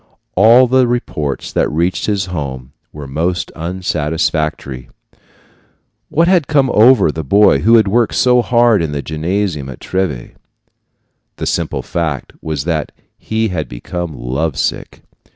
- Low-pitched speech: Yes, very low, 85 Hz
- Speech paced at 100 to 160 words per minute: Yes, average, 140 wpm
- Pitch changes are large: Yes, wide, 6.8 semitones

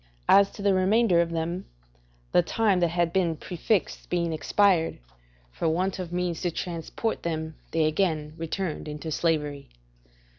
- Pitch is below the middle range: No, medium, 170 Hz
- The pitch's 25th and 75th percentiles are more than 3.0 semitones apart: No, narrow, 2.6 semitones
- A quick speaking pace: No, average, 150 wpm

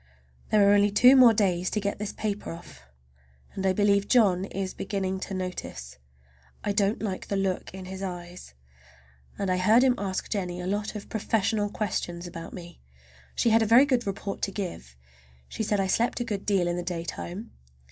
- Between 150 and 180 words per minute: No, average, 195 wpm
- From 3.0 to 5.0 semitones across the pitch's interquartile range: No, narrow, 2.6 semitones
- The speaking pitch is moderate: No, high, 195 Hz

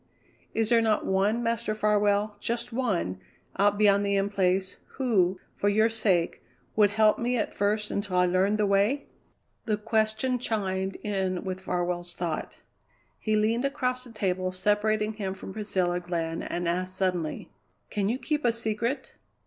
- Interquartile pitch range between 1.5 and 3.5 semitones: Yes, average, 2.9 semitones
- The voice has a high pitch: Yes, high, 205 Hz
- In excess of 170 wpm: No, average, 160 wpm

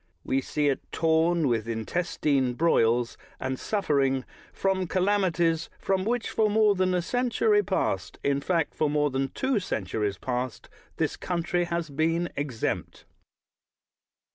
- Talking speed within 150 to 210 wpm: No, average, 140 wpm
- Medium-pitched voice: Yes, medium, 165 Hz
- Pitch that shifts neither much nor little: No, wide, 5.8 semitones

